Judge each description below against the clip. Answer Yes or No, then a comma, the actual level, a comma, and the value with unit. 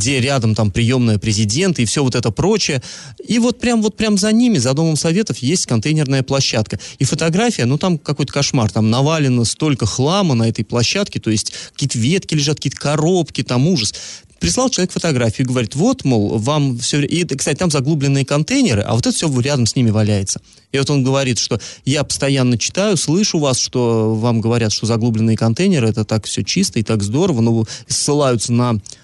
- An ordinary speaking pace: No, fast, 190 wpm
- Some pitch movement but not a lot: No, wide, 5.8 semitones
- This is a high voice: No, low, 135 Hz